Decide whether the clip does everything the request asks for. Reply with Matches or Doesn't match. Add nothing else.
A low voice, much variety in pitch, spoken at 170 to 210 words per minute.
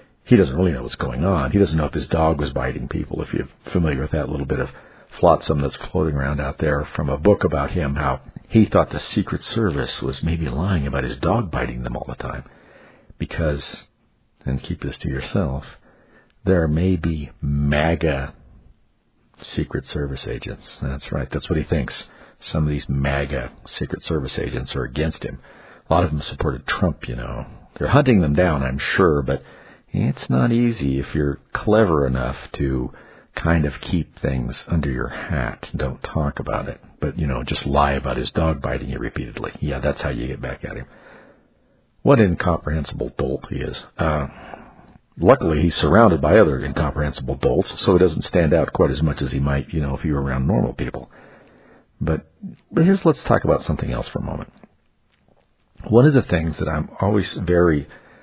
Doesn't match